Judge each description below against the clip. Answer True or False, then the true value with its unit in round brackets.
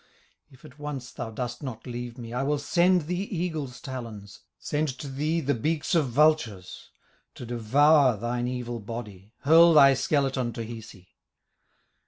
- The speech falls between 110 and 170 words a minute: True (155 wpm)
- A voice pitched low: True (130 Hz)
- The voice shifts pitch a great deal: False (4.2 semitones)